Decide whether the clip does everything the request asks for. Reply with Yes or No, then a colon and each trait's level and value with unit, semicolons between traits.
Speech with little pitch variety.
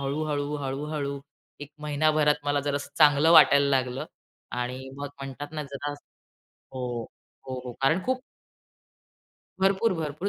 Yes: narrow, 2.0 semitones